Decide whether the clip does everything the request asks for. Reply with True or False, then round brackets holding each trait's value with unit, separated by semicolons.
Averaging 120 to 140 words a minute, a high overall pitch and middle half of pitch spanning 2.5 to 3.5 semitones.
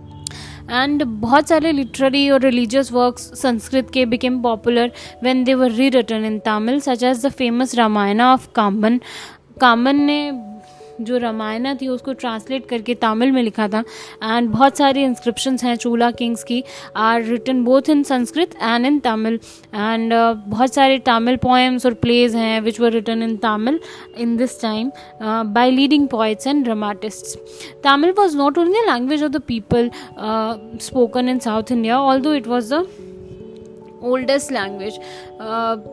False (150 wpm; 245 Hz; 2.9 semitones)